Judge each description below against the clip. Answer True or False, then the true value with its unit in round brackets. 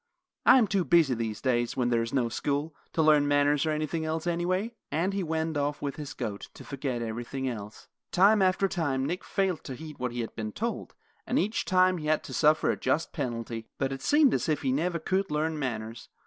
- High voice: False (150 Hz)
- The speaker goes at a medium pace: False (225 wpm)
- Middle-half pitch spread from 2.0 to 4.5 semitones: False (5.4 semitones)